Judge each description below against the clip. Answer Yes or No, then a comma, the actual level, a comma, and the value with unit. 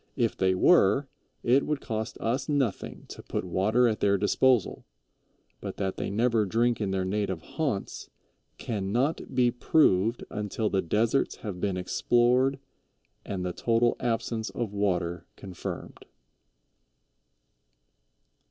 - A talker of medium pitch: No, low, 110 Hz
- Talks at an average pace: No, slow, 130 wpm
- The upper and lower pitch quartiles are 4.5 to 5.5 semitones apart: No, average, 4.0 semitones